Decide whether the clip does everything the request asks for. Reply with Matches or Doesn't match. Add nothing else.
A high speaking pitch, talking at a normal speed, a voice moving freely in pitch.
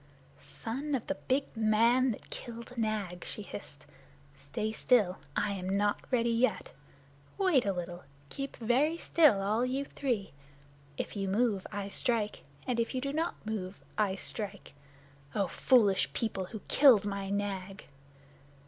Doesn't match